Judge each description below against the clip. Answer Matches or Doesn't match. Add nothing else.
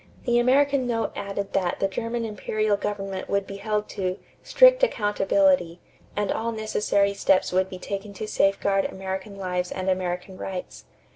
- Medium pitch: Doesn't match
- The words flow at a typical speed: Matches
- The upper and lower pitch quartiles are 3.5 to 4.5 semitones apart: Doesn't match